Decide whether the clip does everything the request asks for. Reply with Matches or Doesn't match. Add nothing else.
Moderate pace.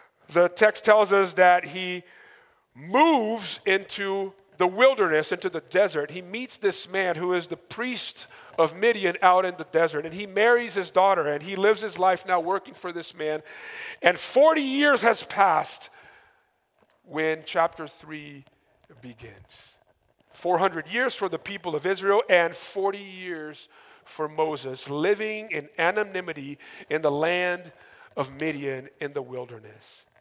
Matches